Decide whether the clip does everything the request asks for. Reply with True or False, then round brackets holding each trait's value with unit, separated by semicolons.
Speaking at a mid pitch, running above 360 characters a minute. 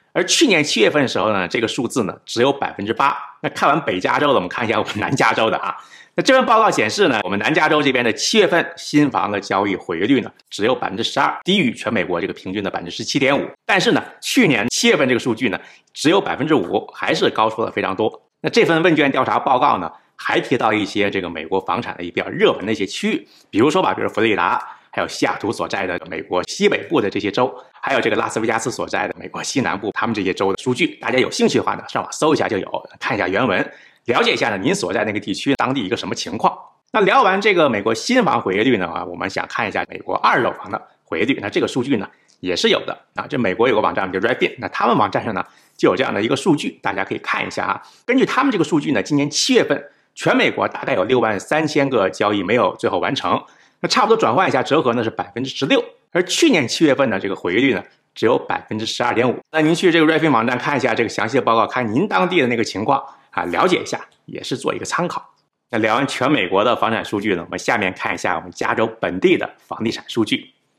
True (155 Hz; 395 characters per minute)